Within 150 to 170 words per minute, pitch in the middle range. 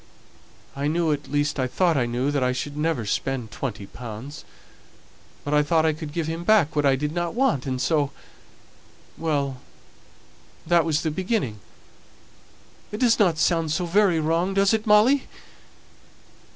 Yes: average, 155 wpm; medium, 155 Hz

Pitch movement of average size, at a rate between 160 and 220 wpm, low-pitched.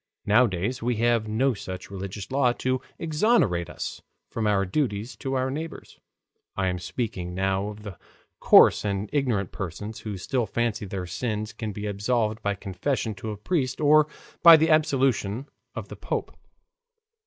Yes: average, 4.9 semitones; average, 165 wpm; low, 110 Hz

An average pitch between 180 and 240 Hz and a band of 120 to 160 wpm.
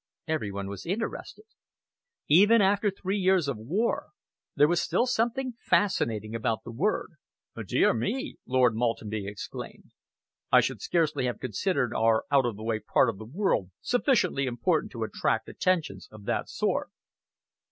No: medium, 140 Hz; average, 150 wpm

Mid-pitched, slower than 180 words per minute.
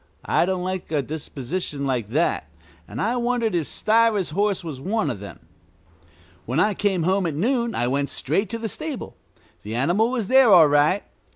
No: medium, 180 Hz; average, 185 wpm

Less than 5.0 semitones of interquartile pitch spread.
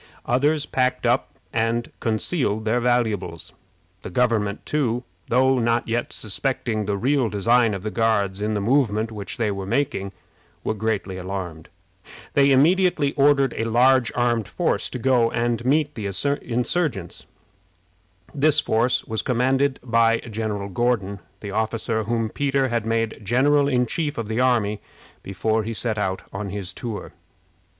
Yes: average, 3.7 semitones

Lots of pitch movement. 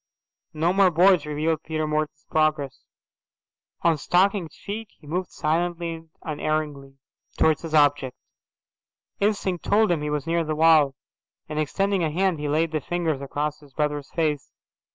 No: narrow, 2.6 semitones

